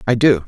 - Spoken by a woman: No, male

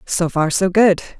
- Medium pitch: Yes, medium, 180 Hz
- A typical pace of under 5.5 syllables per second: Yes, 4.3 syllables/s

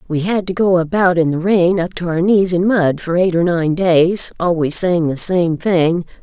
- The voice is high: No, medium, 175 Hz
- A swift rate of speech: Yes, fast, 230 wpm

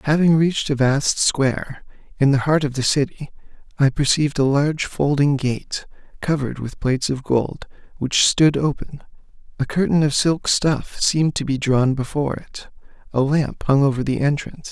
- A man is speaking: Yes, male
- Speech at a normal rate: Yes, average, 170 wpm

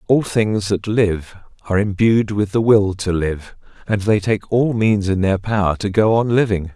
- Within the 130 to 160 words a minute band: No, fast, 205 wpm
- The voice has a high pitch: No, low, 100 Hz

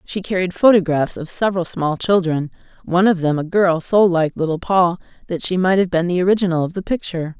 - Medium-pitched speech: Yes, medium, 175 Hz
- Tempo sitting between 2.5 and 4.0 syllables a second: No, 5.9 syllables/s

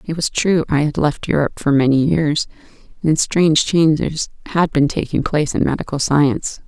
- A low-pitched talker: No, medium, 150 Hz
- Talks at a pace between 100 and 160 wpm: No, average, 180 wpm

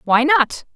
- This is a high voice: Yes, very high, 280 Hz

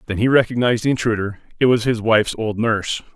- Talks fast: Yes, fast, 210 wpm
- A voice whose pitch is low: Yes, low, 115 Hz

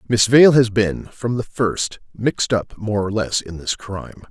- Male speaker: Yes, male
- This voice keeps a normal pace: No, fast, 210 wpm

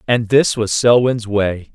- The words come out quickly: No, average, 170 wpm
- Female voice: No, male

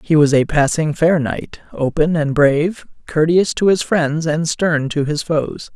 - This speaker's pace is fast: No, average, 190 wpm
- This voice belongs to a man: Yes, male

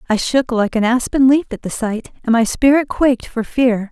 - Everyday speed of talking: No, fast, 230 wpm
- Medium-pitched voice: No, high, 245 Hz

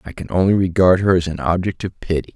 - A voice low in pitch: Yes, very low, 90 Hz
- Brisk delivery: Yes, fast, 255 wpm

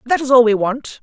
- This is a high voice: Yes, high, 245 Hz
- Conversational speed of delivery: No, fast, 290 wpm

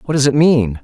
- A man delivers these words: Yes, male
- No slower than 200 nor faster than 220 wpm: No, fast, 285 wpm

